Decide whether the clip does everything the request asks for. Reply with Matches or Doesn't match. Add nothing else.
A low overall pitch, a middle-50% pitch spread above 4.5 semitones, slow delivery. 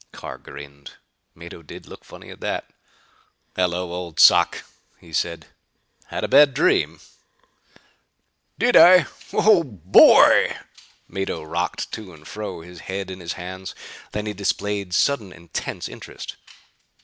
Doesn't match